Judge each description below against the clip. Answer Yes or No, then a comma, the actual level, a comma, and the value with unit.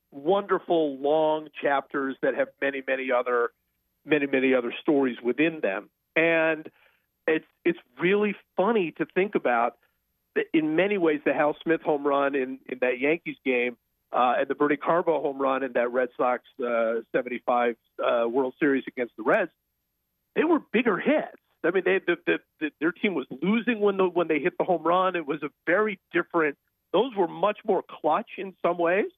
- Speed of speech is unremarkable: Yes, average, 185 wpm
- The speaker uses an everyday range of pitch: No, wide, 6.0 semitones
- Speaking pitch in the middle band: Yes, medium, 155 Hz